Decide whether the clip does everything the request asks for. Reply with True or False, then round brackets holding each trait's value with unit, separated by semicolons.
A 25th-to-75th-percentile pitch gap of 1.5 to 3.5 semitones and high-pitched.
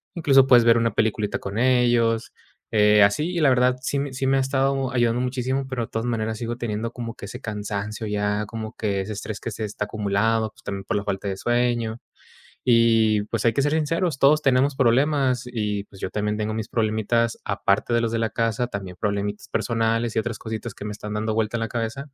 False (2.9 semitones; 115 Hz)